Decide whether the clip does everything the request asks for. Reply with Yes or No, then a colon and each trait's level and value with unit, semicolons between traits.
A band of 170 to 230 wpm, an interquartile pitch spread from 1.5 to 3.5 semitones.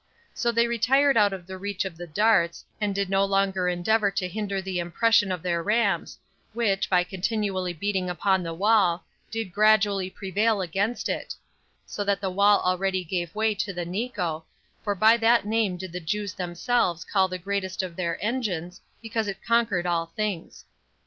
Yes: average, 180 wpm; average, 3.0 semitones